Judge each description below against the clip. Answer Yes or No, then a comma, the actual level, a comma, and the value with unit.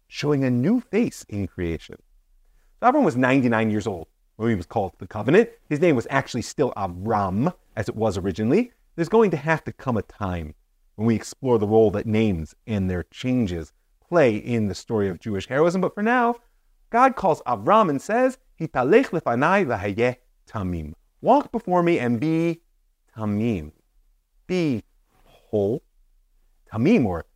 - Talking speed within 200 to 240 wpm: No, average, 165 wpm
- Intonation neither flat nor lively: No, wide, 8.5 semitones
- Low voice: Yes, low, 120 Hz